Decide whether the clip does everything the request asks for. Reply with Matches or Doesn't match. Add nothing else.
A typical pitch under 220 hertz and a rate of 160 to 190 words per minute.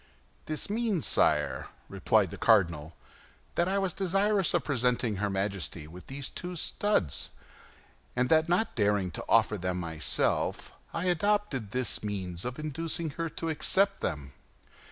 Doesn't match